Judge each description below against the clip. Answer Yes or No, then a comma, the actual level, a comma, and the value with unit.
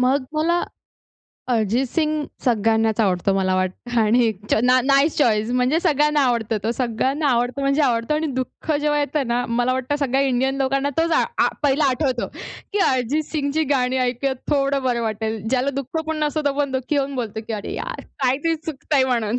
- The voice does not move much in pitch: No, average, 3.4 semitones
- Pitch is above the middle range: Yes, very high, 260 Hz